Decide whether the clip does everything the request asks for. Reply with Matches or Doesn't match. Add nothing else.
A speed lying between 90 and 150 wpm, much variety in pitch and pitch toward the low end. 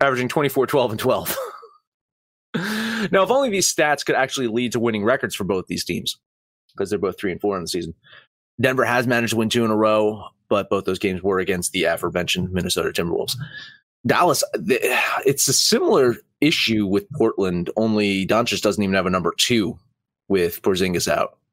Doesn't match